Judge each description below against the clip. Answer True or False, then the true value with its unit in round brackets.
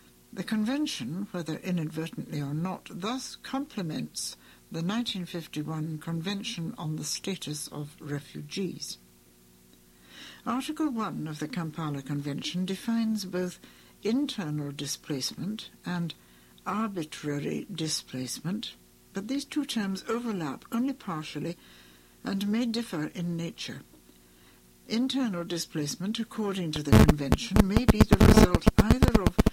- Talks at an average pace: False (110 wpm)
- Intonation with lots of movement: True (6.5 semitones)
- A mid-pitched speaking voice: True (170 Hz)